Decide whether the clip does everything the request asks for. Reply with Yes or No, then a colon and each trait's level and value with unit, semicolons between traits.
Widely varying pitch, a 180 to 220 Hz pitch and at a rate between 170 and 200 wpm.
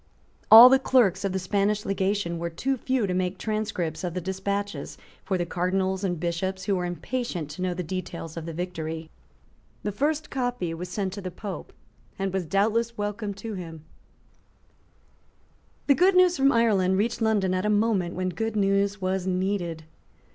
No: average, 3.0 semitones; high, 190 Hz; average, 175 wpm